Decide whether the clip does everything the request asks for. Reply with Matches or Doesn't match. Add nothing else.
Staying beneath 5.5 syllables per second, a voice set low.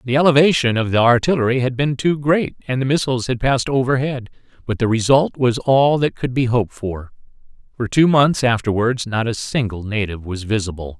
Doesn't match